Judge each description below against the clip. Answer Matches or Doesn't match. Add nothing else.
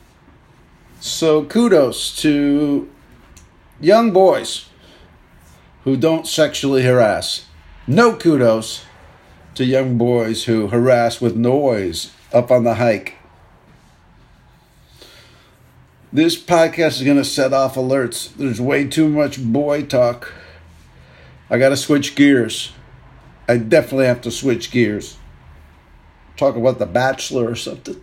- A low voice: Matches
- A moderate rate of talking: Doesn't match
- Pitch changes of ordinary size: Matches